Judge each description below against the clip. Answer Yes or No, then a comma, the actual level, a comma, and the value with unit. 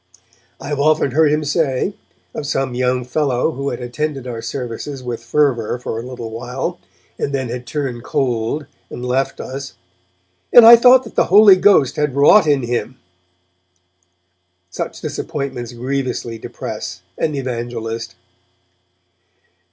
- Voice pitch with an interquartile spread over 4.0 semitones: No, average, 3.5 semitones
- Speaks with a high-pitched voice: No, low, 130 Hz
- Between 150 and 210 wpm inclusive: No, average, 140 wpm